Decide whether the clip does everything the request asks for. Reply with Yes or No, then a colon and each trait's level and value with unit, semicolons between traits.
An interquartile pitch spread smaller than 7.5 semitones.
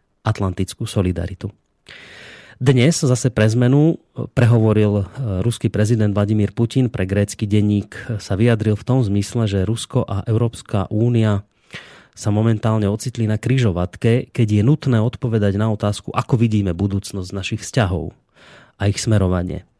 Yes: average, 2.9 semitones